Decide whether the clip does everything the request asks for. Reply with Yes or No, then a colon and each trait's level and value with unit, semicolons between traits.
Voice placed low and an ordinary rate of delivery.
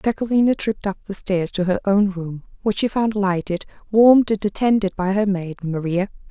No: high, 200 Hz; average, 190 wpm